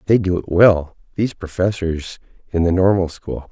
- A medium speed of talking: Yes, average, 170 wpm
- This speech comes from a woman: No, male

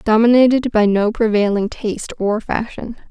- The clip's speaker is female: Yes, female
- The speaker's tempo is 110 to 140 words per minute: Yes, slow, 135 wpm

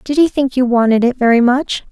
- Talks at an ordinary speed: No, fast, 250 wpm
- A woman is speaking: Yes, female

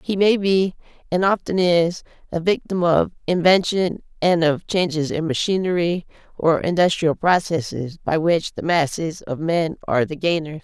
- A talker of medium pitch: Yes, medium, 170 Hz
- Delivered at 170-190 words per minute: No, average, 150 wpm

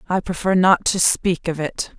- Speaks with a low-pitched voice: No, medium, 175 Hz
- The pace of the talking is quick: Yes, fast, 210 wpm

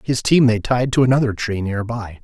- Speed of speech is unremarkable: No, fast, 240 wpm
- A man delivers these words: Yes, male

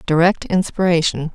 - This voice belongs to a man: No, female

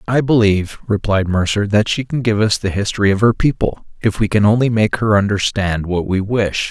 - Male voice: Yes, male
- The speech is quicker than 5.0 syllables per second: Yes, 5.4 syllables/s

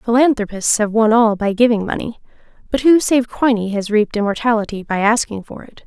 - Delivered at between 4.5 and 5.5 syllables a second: No, 5.7 syllables/s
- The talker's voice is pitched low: No, high, 225 Hz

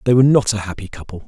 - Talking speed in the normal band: No, fast, 280 wpm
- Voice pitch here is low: Yes, low, 110 Hz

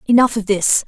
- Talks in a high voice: Yes, high, 215 Hz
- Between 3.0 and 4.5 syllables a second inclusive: No, 5.5 syllables/s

